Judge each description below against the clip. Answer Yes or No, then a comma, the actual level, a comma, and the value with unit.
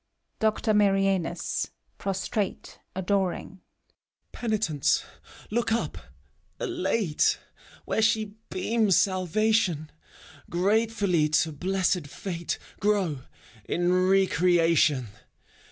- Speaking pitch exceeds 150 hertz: Yes, high, 190 Hz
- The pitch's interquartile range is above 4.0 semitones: No, average, 3.7 semitones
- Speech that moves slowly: Yes, slow, 75 wpm